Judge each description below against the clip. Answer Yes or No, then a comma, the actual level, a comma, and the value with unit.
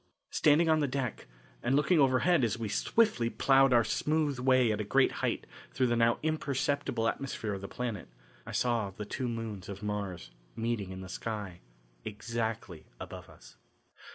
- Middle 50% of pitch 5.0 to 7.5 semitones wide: No, average, 4.6 semitones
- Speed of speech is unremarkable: Yes, average, 170 wpm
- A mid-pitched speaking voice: No, low, 115 Hz